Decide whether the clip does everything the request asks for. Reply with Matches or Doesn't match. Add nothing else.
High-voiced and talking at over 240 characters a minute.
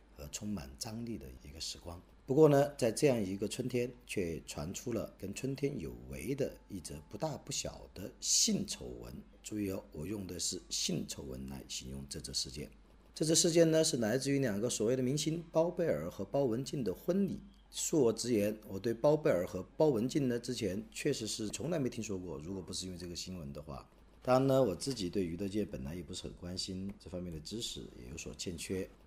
Doesn't match